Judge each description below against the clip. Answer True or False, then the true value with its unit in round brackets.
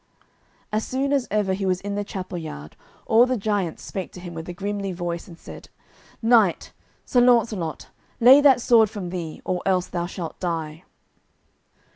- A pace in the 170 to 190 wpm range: True (175 wpm)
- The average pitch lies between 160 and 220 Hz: True (190 Hz)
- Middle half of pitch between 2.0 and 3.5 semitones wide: False (4.2 semitones)